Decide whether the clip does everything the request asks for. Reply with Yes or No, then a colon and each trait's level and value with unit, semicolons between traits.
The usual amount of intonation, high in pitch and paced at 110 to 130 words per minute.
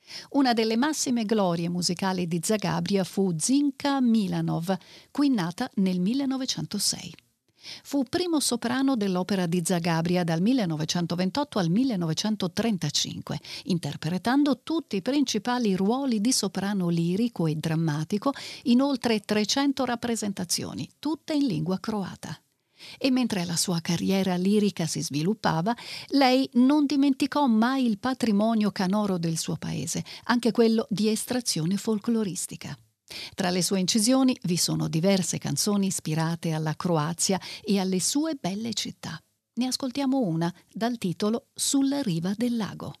No: wide, 5.8 semitones; high, 205 Hz; average, 125 wpm